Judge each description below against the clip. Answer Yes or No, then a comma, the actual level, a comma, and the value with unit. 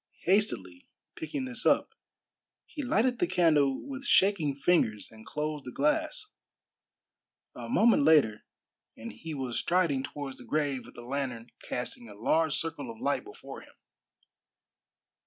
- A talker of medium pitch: Yes, medium, 150 Hz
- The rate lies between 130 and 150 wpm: Yes, average, 140 wpm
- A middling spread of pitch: No, wide, 7.7 semitones